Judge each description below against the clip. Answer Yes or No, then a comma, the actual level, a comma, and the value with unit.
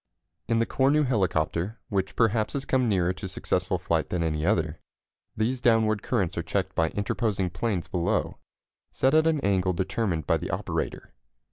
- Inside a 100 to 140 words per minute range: No, average, 165 wpm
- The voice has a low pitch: Yes, low, 100 Hz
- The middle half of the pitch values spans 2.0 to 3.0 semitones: No, average, 4.4 semitones